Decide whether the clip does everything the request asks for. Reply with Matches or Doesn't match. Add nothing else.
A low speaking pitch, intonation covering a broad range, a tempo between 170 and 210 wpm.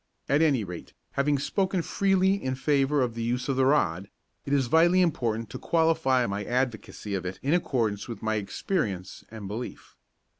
Matches